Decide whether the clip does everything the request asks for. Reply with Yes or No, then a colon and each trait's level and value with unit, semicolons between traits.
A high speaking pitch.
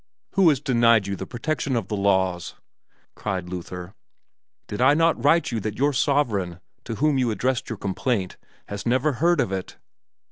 No: low, 115 Hz